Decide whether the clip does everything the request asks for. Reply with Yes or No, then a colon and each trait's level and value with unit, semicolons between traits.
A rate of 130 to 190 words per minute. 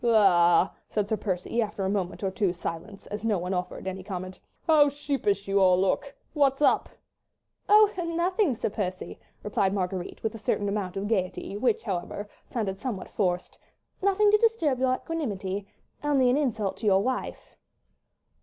Yes: average, 165 wpm